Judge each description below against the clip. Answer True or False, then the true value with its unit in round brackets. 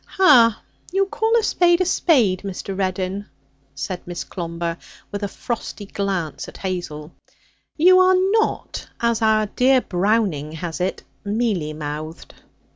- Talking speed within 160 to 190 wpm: False (135 wpm)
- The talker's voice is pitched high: True (200 Hz)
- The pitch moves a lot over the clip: True (6.7 semitones)